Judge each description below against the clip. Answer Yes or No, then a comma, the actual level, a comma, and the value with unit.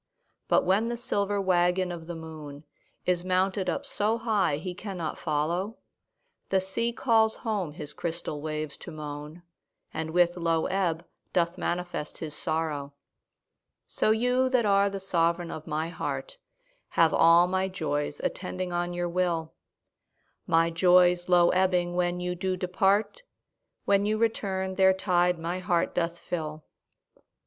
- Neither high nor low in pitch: Yes, medium, 180 Hz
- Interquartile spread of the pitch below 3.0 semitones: Yes, narrow, 2.6 semitones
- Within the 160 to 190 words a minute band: No, average, 145 wpm